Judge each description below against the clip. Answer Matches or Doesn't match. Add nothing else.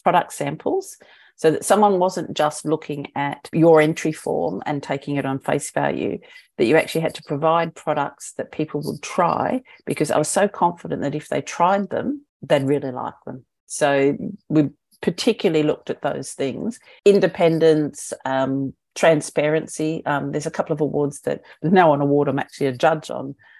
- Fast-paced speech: Doesn't match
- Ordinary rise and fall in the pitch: Matches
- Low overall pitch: Doesn't match